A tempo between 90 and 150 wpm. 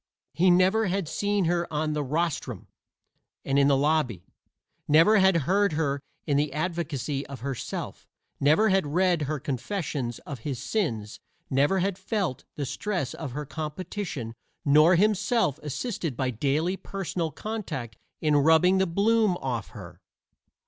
Yes: average, 140 wpm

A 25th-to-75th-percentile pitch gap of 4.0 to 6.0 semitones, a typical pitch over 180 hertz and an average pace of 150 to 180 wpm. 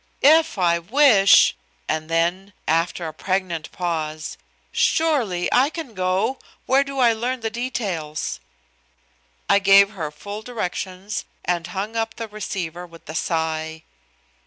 No: average, 5.3 semitones; high, 190 Hz; slow, 135 wpm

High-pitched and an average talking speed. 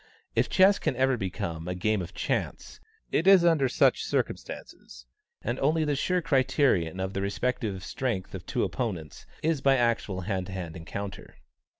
No: low, 110 Hz; average, 170 wpm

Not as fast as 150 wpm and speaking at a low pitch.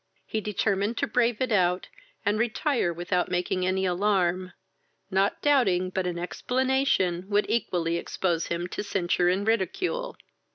No: average, 140 wpm; high, 190 Hz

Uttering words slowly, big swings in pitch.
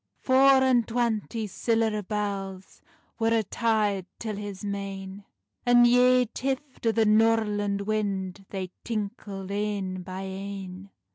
No: slow, 125 wpm; average, 2.7 semitones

